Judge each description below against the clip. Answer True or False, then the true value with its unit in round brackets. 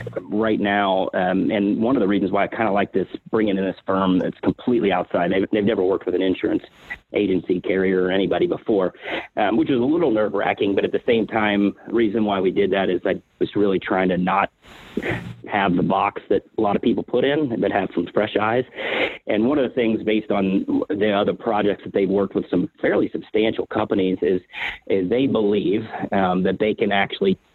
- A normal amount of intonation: False (2.1 semitones)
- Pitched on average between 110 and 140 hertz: False (100 Hz)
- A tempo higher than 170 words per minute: True (205 wpm)